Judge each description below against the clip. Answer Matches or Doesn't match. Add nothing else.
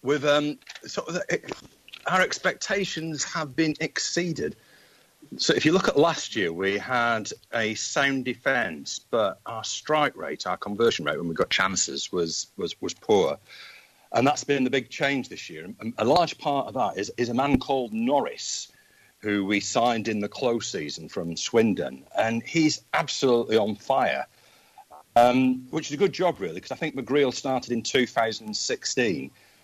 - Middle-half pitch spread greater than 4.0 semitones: Matches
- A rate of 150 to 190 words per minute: Matches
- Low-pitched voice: Matches